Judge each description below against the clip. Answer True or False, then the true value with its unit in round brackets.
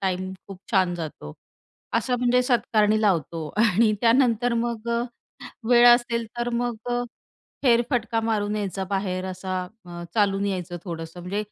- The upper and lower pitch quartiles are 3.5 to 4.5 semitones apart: True (4.1 semitones)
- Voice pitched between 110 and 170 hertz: False (215 Hz)